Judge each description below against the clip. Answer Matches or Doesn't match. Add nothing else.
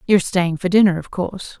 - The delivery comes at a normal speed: Doesn't match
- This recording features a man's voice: Doesn't match